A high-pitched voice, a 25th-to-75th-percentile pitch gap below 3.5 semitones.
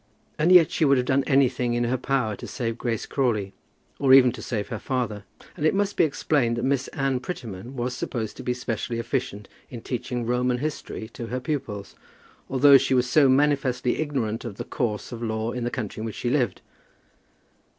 No: low, 125 Hz; average, 2.9 semitones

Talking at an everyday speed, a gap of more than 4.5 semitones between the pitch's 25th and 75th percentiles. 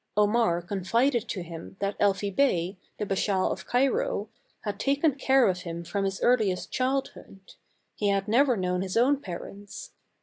Yes: average, 160 wpm; average, 5.3 semitones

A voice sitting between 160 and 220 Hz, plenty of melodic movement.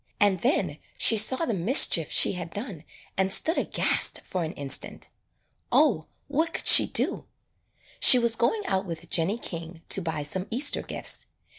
Yes: high, 190 Hz; wide, 6.5 semitones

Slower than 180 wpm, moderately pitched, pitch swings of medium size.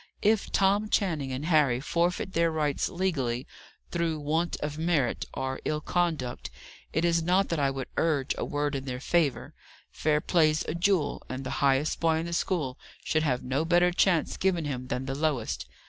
No: average, 185 wpm; medium, 155 Hz; average, 4.0 semitones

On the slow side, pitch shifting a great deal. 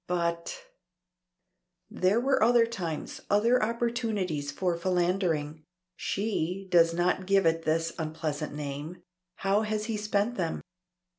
No: slow, 120 wpm; average, 4.6 semitones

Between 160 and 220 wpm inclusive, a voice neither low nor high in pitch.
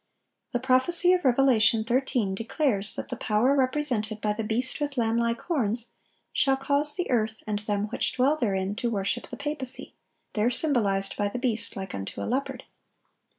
No: average, 170 wpm; high, 240 Hz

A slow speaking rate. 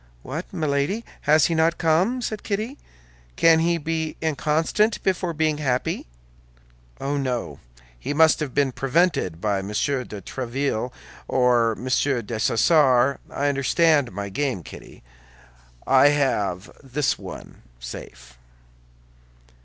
Yes: slow, 120 wpm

